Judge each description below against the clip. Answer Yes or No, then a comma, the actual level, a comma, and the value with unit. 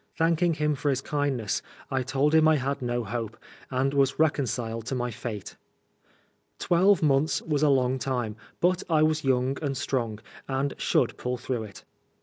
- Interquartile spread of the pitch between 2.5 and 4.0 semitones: Yes, average, 3.6 semitones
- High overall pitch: No, low, 135 Hz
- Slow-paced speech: No, average, 170 wpm